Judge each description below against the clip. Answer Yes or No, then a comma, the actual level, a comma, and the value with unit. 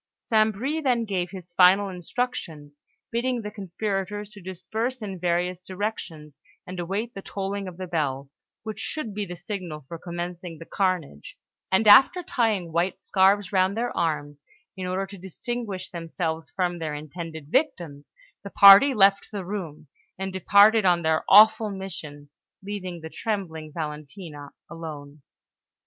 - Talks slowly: No, average, 150 wpm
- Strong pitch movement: No, average, 3.9 semitones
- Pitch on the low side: No, medium, 185 Hz